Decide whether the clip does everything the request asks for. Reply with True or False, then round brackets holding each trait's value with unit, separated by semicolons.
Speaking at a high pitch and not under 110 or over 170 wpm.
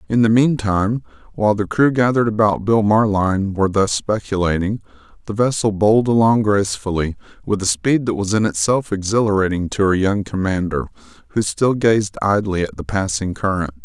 False (100 Hz; 165 wpm)